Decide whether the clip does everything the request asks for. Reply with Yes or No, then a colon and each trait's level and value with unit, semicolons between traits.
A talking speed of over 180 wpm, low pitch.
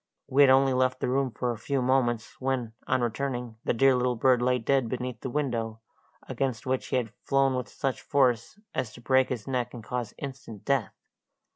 Yes: fast, 205 wpm; low, 125 Hz